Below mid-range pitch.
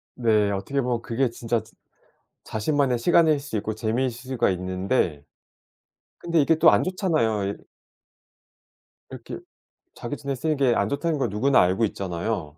Yes: low, 120 Hz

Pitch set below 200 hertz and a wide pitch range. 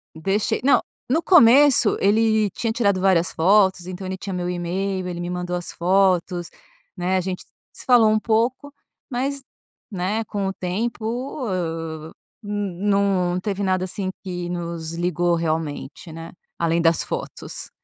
No: medium, 185 Hz; average, 3.4 semitones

